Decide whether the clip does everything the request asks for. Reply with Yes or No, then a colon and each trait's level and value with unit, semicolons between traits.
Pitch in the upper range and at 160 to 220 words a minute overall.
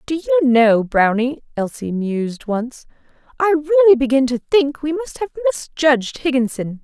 No: very high, 275 Hz; average, 150 wpm